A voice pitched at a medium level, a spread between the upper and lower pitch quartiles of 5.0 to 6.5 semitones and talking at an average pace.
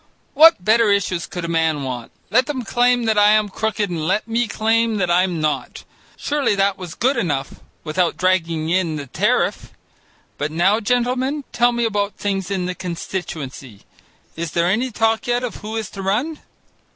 No: high, 200 Hz; average, 5.3 semitones; average, 180 wpm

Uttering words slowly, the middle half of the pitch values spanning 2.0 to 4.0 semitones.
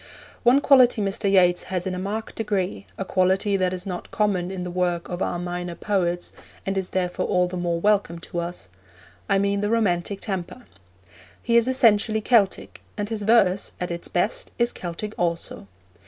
No: average, 185 wpm; average, 3.0 semitones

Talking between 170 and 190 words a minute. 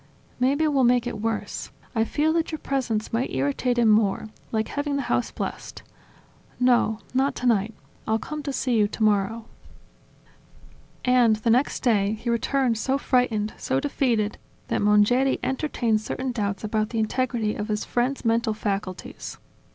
No: average, 160 wpm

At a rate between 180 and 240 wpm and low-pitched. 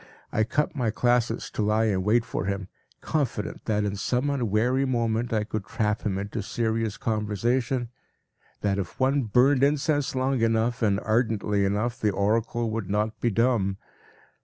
No: average, 160 wpm; low, 115 Hz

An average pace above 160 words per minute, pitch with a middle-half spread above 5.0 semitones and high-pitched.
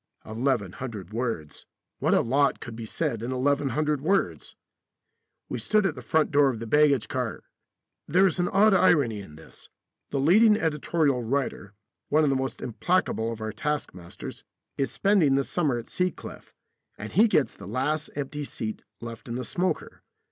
No: average, 175 wpm; wide, 5.4 semitones; medium, 140 Hz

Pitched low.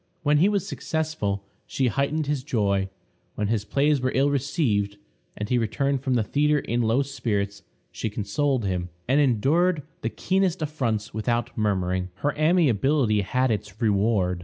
Yes: low, 125 Hz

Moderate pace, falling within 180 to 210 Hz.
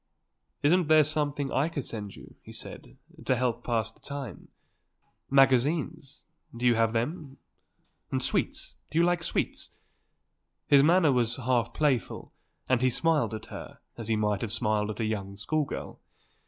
No: average, 170 wpm; low, 130 Hz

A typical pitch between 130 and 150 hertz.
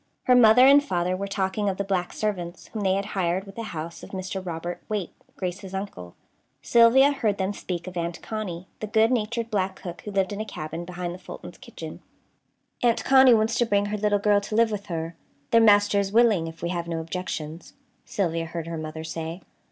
No: high, 195 Hz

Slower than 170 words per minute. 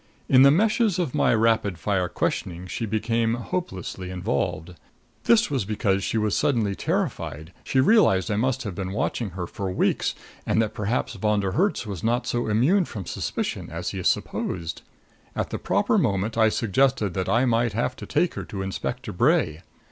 No: average, 180 wpm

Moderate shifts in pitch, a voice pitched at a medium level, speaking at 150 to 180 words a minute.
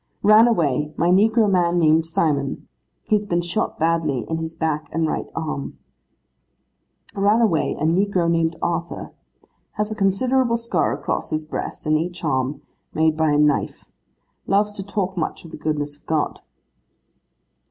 Yes: average, 4.4 semitones; medium, 165 Hz; average, 160 wpm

